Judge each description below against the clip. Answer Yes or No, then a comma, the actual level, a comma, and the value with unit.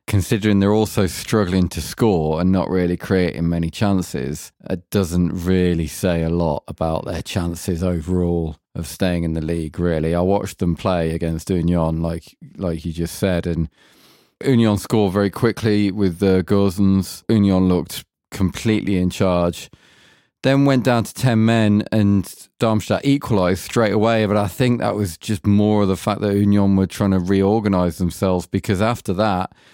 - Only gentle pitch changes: No, average, 3.3 semitones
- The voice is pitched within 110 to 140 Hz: No, very low, 95 Hz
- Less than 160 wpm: No, average, 165 wpm